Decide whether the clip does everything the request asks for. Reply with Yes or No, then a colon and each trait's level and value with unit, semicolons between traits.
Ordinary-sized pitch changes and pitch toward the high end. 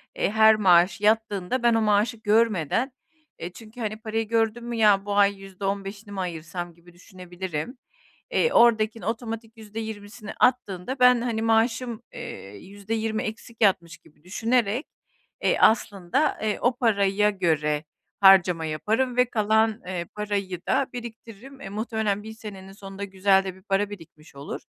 Yes: average, 3.0 semitones; high, 210 Hz